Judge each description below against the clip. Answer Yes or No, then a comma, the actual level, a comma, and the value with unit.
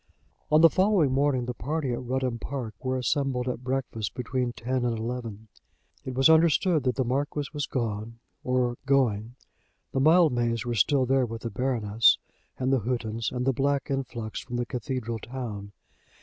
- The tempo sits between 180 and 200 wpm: No, average, 170 wpm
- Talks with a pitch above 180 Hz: No, low, 125 Hz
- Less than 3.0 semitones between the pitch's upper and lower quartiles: Yes, narrow, 2.6 semitones